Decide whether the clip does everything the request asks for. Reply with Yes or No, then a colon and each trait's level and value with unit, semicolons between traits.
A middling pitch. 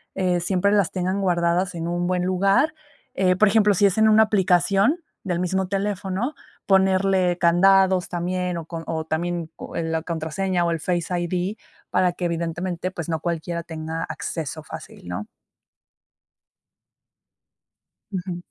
Yes: medium, 180 Hz